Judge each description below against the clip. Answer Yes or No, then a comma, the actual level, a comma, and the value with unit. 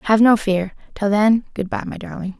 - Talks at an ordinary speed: No, fast, 225 wpm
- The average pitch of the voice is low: No, high, 210 Hz